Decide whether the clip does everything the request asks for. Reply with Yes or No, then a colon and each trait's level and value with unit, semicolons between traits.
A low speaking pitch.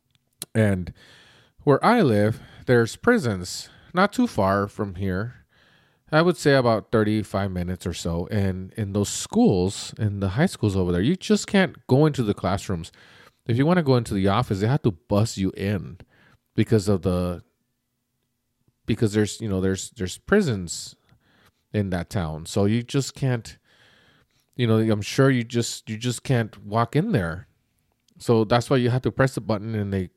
Yes: low, 110 Hz